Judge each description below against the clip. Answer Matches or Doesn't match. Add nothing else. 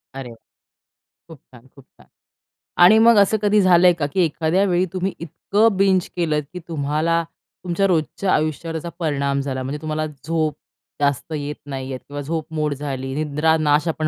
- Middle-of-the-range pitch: Matches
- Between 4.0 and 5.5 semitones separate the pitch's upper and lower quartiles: Doesn't match